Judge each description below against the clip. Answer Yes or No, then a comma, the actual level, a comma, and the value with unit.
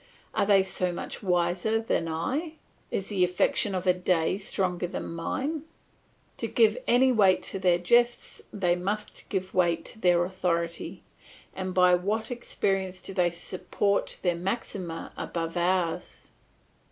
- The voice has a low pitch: No, medium, 185 Hz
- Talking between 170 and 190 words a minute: No, average, 145 wpm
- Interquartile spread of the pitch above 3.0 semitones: No, average, 2.7 semitones